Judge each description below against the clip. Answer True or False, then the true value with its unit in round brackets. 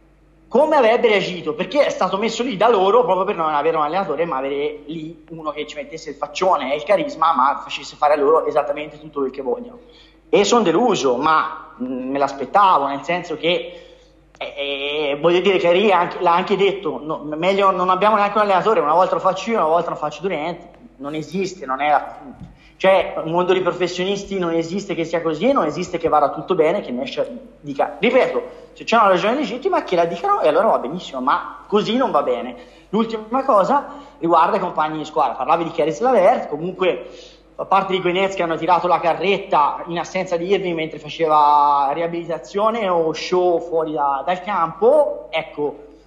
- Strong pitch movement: False (4.0 semitones)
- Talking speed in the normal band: False (195 wpm)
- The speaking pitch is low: False (170 Hz)